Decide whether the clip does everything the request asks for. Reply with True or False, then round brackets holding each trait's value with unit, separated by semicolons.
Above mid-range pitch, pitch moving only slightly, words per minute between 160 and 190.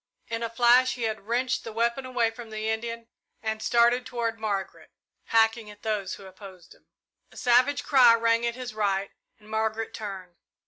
True (225 Hz; 1.7 semitones; 180 wpm)